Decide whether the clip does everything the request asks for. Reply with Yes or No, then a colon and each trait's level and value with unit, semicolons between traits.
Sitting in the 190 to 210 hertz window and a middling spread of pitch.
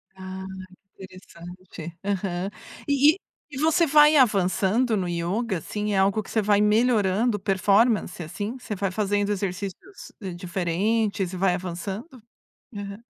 Yes: high, 200 Hz; average, 3.2 semitones